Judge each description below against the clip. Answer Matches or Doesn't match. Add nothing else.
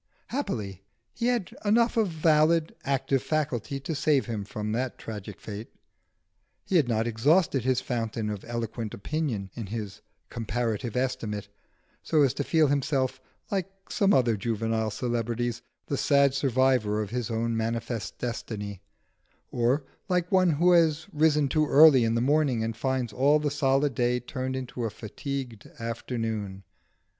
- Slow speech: Doesn't match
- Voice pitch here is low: Matches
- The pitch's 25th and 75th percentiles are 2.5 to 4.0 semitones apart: Doesn't match